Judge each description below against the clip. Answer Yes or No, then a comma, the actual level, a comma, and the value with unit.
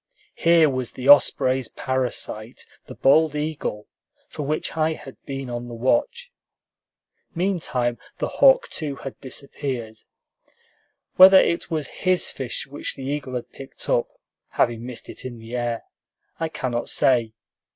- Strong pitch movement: No, average, 4.4 semitones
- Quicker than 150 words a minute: No, average, 140 wpm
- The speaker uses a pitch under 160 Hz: Yes, low, 135 Hz